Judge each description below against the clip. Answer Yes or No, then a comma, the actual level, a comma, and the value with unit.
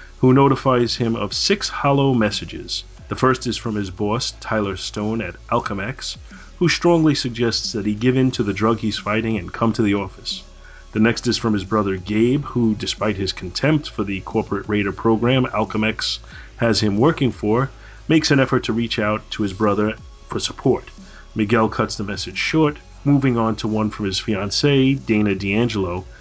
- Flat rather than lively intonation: No, average, 3.4 semitones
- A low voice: Yes, low, 110 Hz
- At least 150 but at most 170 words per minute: No, average, 185 wpm